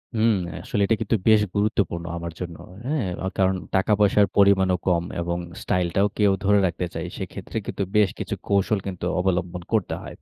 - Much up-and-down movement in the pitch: No, average, 2.7 semitones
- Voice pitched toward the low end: Yes, very low, 95 Hz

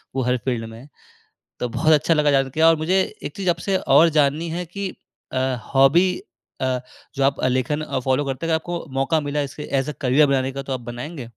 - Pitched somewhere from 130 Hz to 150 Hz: Yes, medium, 140 Hz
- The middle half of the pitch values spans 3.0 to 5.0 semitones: Yes, average, 3.5 semitones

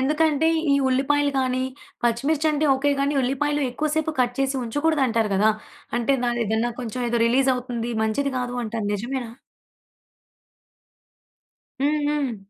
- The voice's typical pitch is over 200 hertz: Yes, very high, 260 Hz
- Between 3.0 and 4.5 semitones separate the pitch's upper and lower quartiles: Yes, average, 3.5 semitones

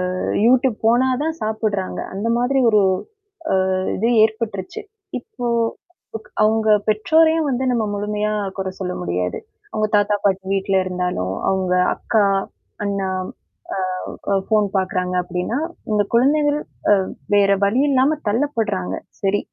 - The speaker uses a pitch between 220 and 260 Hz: No, high, 210 Hz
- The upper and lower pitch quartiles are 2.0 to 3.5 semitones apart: No, average, 4.2 semitones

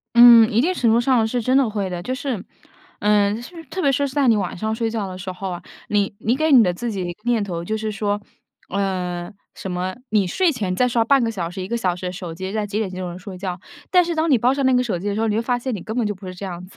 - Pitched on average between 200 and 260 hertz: Yes, high, 210 Hz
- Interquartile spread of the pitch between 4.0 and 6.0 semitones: Yes, average, 4.6 semitones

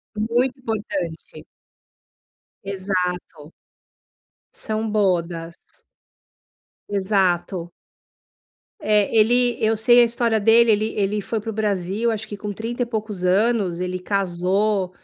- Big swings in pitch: No, average, 3.4 semitones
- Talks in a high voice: Yes, high, 205 Hz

